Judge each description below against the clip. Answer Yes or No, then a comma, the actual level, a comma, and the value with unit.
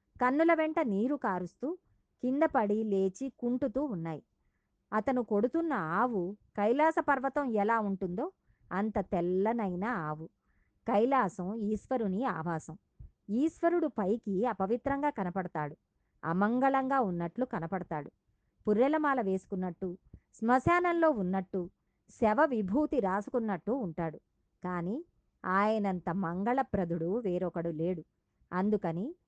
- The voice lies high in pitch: Yes, high, 210 Hz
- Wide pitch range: Yes, wide, 6.1 semitones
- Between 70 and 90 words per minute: Yes, average, 85 wpm